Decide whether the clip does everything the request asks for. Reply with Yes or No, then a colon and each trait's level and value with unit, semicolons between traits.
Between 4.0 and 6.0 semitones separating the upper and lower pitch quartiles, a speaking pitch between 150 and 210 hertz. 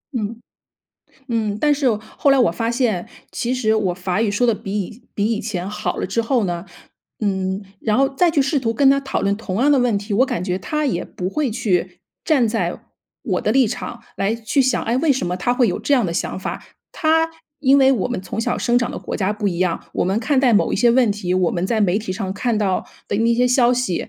No: average, 4.6 semitones; high, 225 Hz